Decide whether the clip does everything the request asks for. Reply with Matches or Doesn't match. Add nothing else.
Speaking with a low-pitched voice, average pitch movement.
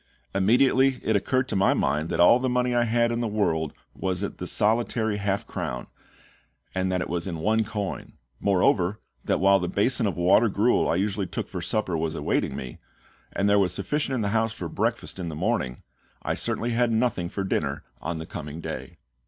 Matches